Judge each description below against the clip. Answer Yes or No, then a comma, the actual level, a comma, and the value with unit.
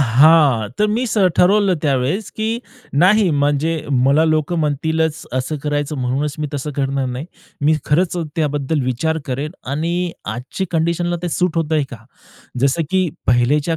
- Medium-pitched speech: Yes, medium, 155 Hz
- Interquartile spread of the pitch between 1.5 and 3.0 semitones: No, average, 3.6 semitones